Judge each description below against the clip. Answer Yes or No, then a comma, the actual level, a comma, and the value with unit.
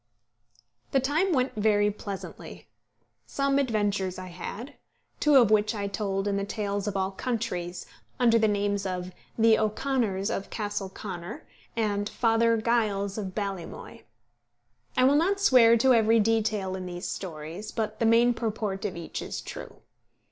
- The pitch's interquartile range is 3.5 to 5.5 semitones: No, average, 2.9 semitones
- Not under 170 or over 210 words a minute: No, average, 155 wpm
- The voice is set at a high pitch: Yes, high, 210 Hz